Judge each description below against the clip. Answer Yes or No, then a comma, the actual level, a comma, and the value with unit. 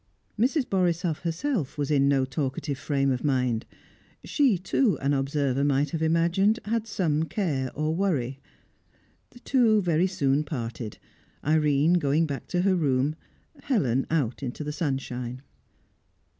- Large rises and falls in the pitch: No, average, 4.8 semitones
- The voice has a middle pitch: Yes, medium, 150 Hz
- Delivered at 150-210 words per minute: No, average, 140 wpm